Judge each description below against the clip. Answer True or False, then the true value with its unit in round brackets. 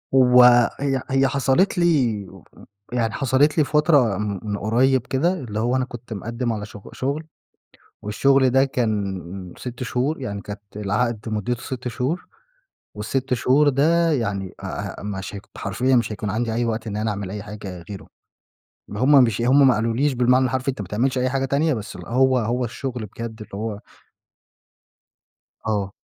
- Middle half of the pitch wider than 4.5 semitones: False (4.0 semitones)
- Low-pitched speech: True (120 Hz)